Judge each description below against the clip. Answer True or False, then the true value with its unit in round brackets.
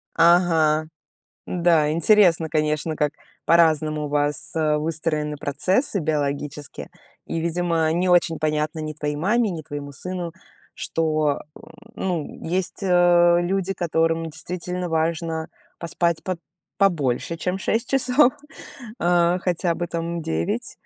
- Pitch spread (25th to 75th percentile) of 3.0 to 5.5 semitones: False (2.5 semitones)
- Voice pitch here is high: False (165 Hz)